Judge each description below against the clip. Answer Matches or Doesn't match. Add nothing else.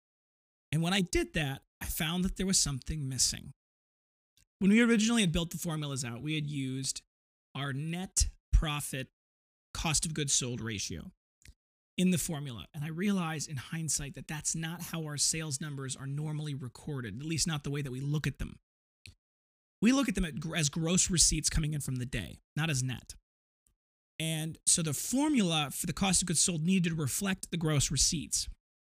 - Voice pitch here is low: Doesn't match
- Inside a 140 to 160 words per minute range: Doesn't match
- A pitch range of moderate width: Matches